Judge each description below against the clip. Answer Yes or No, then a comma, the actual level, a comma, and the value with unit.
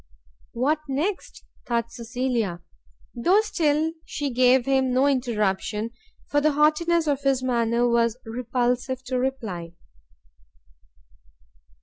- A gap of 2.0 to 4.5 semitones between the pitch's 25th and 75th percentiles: Yes, average, 3.4 semitones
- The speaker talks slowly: Yes, slow, 105 wpm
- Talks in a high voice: Yes, very high, 255 Hz